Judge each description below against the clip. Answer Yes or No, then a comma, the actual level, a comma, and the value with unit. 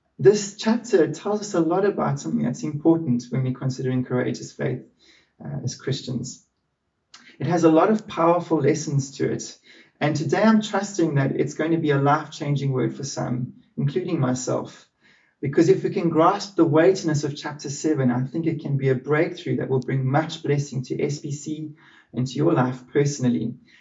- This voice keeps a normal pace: Yes, average, 185 wpm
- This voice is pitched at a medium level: Yes, medium, 150 Hz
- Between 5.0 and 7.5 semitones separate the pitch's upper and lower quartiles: No, average, 4.0 semitones